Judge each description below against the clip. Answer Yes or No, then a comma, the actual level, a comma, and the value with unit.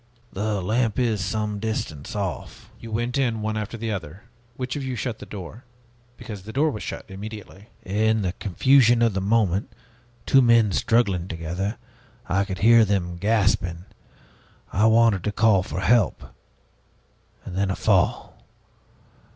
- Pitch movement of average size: Yes, average, 3.3 semitones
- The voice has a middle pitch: No, low, 105 Hz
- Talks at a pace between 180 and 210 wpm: No, average, 150 wpm